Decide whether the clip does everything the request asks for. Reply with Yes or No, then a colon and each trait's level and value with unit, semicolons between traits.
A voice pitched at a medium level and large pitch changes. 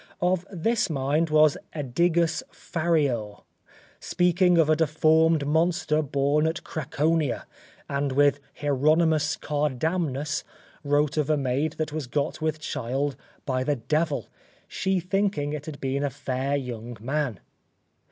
No: medium, 150 Hz; narrow, 2.5 semitones